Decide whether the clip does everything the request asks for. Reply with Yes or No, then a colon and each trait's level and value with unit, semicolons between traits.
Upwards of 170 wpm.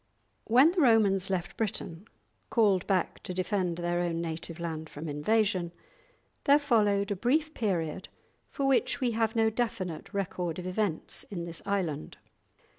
No: average, 150 wpm